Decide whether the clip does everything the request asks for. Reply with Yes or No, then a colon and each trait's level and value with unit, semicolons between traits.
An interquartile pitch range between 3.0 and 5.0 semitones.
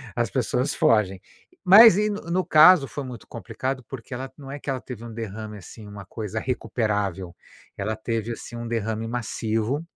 Yes: average, 3.8 semitones